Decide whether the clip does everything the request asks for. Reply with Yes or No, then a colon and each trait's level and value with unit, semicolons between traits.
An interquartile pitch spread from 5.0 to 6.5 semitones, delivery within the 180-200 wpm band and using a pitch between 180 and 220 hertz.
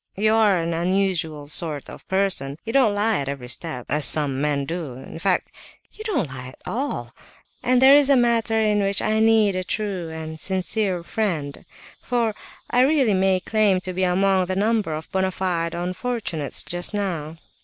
Yes: average, 5.3 semitones; average, 185 wpm; high, 190 Hz